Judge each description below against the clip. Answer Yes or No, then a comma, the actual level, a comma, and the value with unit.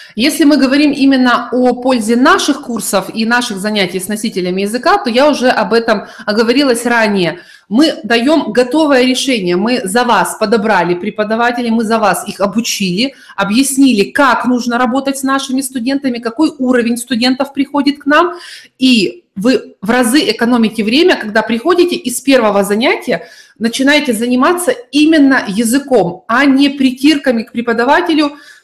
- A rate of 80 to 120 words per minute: No, average, 140 wpm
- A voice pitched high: Yes, high, 245 Hz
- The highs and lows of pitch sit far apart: No, average, 3.5 semitones